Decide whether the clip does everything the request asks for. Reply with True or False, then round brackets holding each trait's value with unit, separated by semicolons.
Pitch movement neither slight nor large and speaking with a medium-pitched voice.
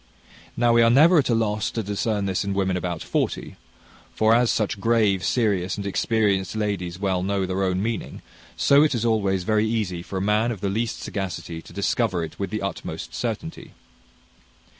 False (3.1 semitones; 100 Hz)